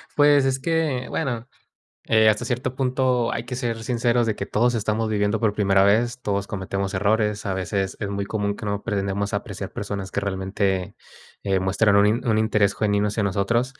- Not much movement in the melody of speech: No, average, 3.0 semitones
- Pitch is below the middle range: Yes, low, 105 Hz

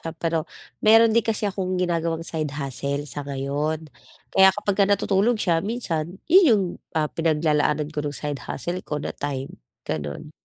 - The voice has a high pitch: No, medium, 160 Hz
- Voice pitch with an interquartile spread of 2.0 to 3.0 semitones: No, average, 4.5 semitones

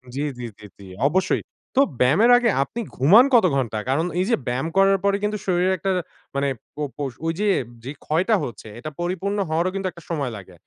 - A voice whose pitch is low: No, medium, 170 Hz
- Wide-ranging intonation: Yes, wide, 6.2 semitones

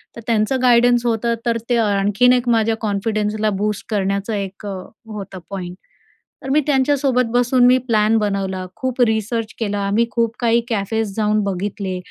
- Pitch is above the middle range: Yes, high, 220 Hz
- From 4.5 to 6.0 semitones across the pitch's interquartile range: No, average, 3.0 semitones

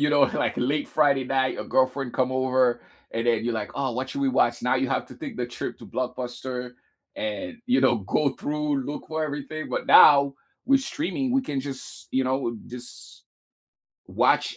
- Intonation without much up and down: No, average, 3.3 semitones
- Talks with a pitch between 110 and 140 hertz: Yes, low, 135 Hz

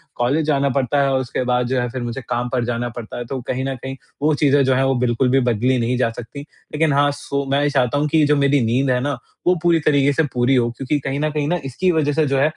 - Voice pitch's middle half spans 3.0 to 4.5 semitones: No, narrow, 2.6 semitones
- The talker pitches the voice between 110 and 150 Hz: Yes, low, 135 Hz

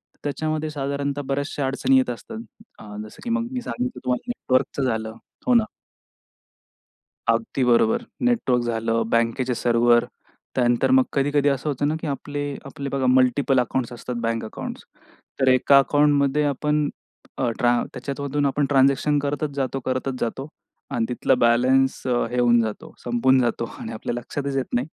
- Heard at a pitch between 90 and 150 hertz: Yes, low, 135 Hz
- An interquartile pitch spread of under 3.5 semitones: Yes, average, 3.0 semitones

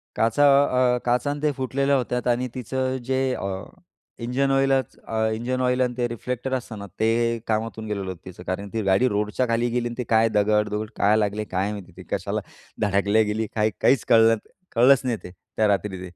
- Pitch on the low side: Yes, low, 115 Hz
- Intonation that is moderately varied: Yes, average, 3.2 semitones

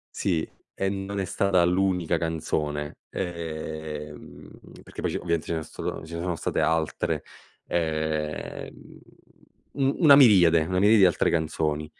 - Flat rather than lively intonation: No, average, 3.2 semitones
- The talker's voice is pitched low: Yes, very low, 85 Hz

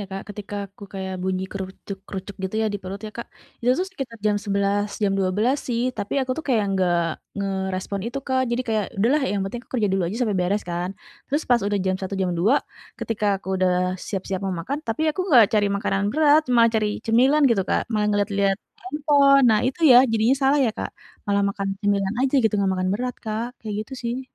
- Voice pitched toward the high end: Yes, high, 210 Hz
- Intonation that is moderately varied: Yes, average, 4.0 semitones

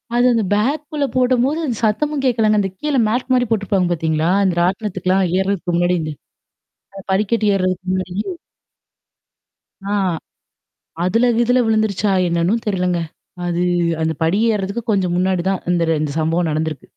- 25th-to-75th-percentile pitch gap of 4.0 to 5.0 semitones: Yes, average, 4.5 semitones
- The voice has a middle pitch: No, high, 195 Hz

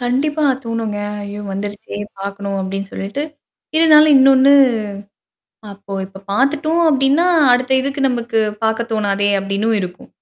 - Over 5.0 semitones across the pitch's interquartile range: Yes, wide, 5.5 semitones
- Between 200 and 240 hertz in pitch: Yes, high, 230 Hz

